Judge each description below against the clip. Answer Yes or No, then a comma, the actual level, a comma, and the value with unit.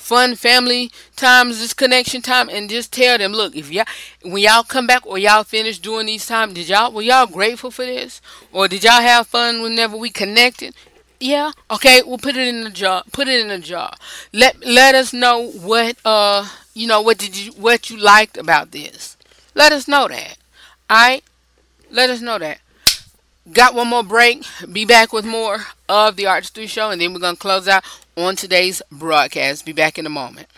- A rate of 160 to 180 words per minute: No, average, 200 wpm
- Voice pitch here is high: Yes, high, 230 Hz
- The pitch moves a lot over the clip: No, average, 3.6 semitones